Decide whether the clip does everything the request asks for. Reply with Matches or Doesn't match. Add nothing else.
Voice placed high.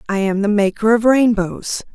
Matches